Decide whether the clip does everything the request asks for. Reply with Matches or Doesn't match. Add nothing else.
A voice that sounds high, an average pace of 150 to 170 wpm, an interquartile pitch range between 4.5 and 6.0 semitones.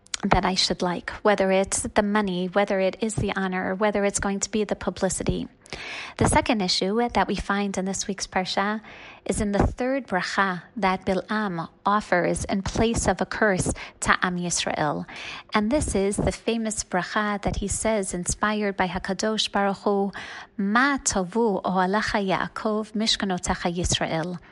Doesn't match